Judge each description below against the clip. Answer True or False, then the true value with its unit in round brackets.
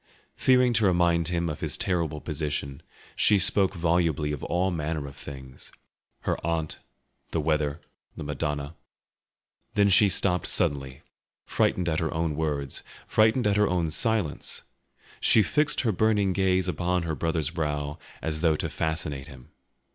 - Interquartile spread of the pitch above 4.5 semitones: False (3.9 semitones)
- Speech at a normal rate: True (145 wpm)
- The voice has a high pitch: False (80 Hz)